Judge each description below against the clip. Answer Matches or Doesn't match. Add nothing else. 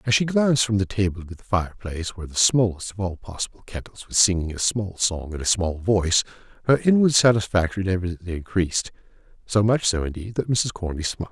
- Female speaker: Doesn't match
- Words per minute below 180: Doesn't match